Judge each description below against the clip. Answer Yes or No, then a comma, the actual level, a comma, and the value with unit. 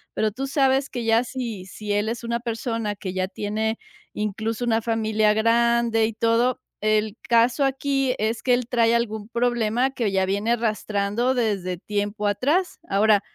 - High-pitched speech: Yes, high, 225 Hz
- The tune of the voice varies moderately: No, narrow, 2.3 semitones